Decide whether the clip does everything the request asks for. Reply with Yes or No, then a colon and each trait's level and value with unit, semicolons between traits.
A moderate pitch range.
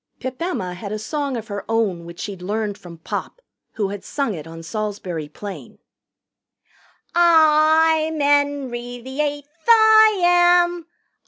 No: wide, 7.9 semitones